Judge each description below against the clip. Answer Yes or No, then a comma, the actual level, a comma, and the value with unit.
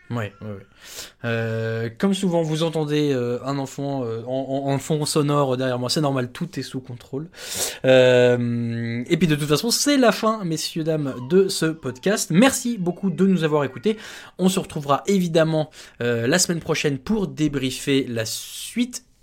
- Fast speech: No, average, 175 wpm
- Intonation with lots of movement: Yes, wide, 5.7 semitones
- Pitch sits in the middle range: Yes, medium, 150 Hz